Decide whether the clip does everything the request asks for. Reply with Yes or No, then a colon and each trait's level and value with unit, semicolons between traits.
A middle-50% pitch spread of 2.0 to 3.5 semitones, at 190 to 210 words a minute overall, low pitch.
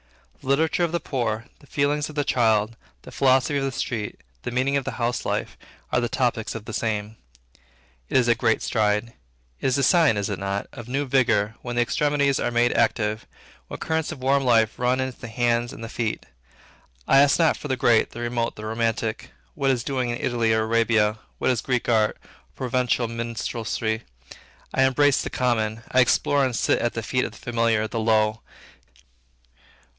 Yes: average, 2.9 semitones; average, 200 wpm; low, 120 Hz